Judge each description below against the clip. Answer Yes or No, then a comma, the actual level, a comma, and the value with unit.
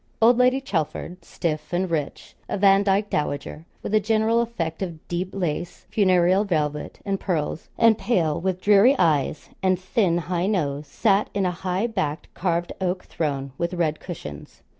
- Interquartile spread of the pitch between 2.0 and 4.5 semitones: Yes, average, 3.8 semitones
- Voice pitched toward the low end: No, medium, 180 Hz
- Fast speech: No, average, 160 wpm